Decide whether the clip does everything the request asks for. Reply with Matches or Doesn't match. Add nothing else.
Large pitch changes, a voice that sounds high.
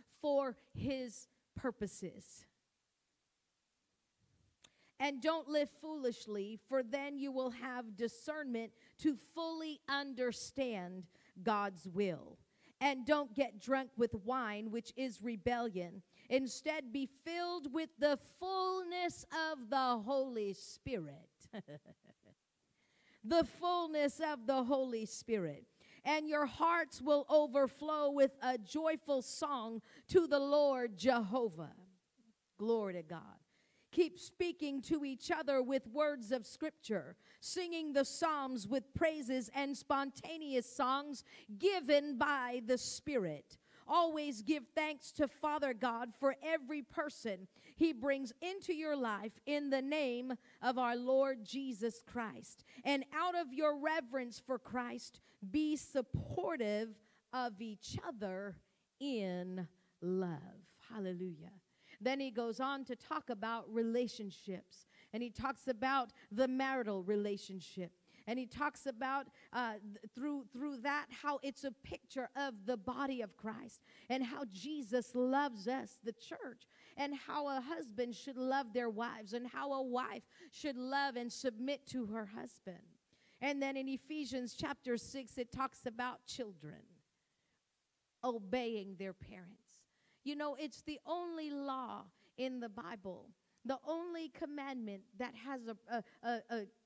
Doesn't match